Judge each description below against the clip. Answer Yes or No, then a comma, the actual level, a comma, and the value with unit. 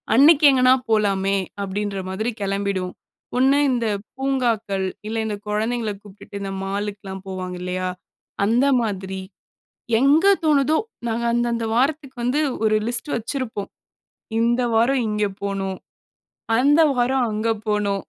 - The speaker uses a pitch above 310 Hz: No, high, 220 Hz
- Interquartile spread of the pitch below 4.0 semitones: No, average, 4.3 semitones